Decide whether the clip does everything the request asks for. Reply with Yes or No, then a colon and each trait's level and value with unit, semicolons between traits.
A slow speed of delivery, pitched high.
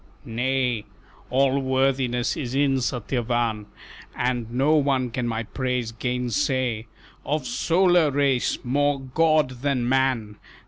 No: slow, 110 wpm; low, 130 Hz